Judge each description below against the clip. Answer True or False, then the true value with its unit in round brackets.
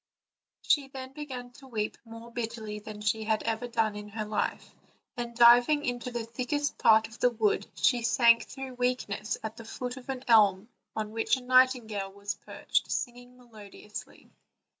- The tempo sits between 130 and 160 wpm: False (175 wpm)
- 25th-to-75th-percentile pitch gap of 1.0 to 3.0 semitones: True (2.5 semitones)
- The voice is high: True (235 Hz)